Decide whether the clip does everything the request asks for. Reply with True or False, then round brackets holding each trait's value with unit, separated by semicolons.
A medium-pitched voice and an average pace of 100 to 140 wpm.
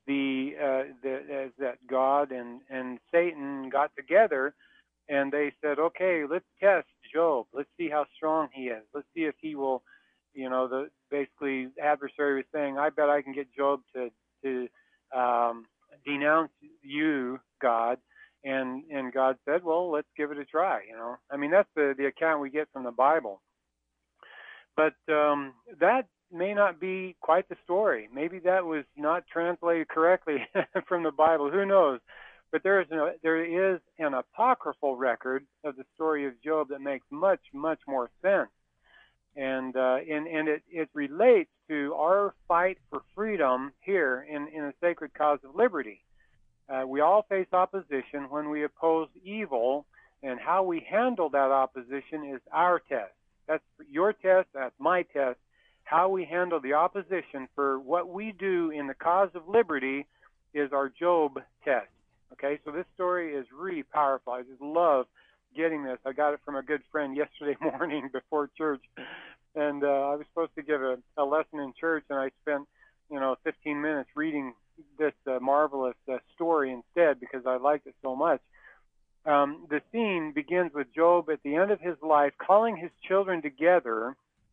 False (150 Hz; 170 wpm)